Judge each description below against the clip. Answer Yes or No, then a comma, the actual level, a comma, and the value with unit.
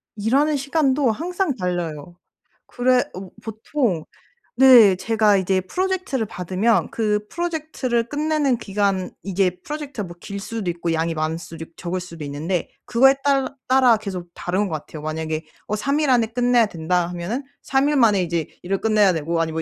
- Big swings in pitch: Yes, wide, 6.9 semitones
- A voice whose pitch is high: Yes, high, 210 Hz